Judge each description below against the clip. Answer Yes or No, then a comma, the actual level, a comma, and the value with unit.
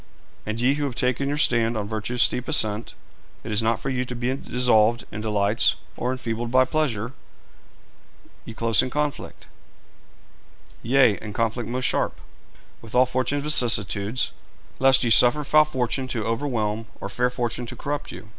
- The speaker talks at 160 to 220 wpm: Yes, average, 165 wpm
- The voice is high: No, low, 120 Hz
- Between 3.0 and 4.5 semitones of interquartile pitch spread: No, narrow, 2.6 semitones